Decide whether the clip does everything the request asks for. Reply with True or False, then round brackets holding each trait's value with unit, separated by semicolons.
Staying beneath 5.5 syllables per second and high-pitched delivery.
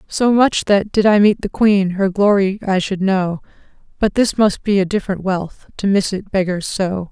True (4.7 syllables/s; 195 Hz)